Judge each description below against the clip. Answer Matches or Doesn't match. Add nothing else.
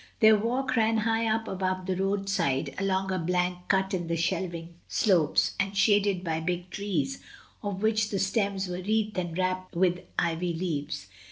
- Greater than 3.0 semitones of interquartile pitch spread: Doesn't match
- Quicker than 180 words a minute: Doesn't match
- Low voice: Doesn't match